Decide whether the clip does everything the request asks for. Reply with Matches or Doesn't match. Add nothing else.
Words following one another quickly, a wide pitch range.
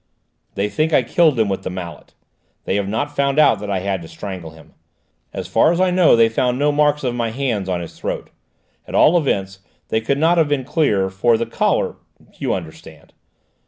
Matches